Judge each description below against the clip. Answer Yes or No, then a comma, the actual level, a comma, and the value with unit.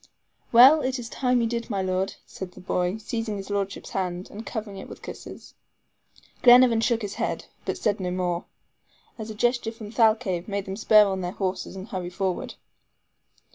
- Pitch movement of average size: Yes, average, 3.4 semitones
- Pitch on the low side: No, high, 205 Hz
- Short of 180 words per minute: No, average, 185 wpm